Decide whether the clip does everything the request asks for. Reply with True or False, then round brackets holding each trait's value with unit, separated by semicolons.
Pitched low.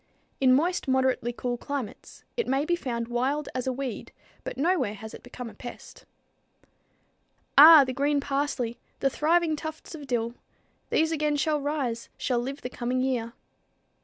False (265 Hz)